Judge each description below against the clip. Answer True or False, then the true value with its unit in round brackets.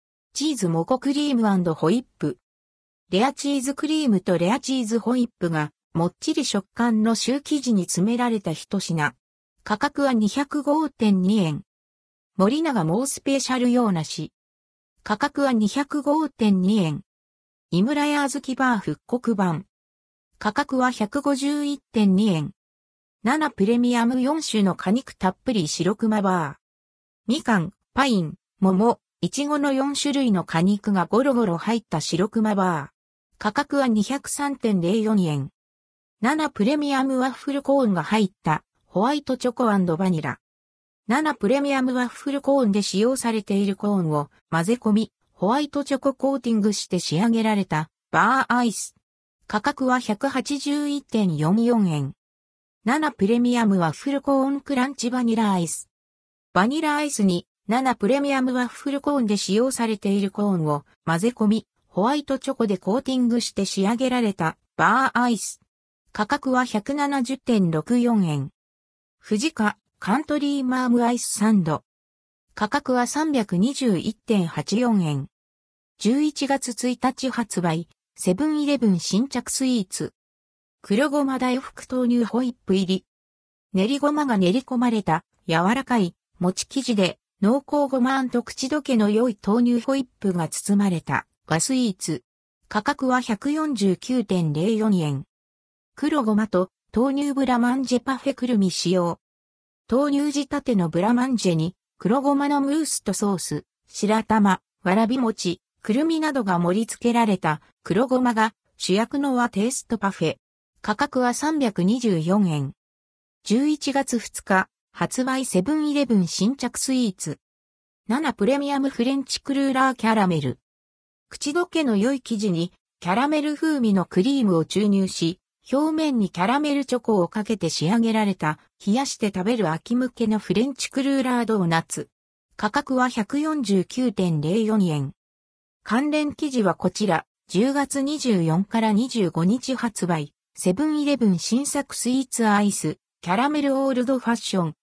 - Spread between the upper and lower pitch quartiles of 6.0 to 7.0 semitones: True (6.6 semitones)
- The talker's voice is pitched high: True (220 Hz)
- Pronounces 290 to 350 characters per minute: False (270 characters per minute)